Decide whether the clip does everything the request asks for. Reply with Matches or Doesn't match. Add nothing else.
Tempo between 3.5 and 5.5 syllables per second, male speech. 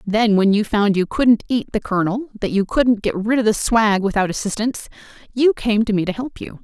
Doesn't match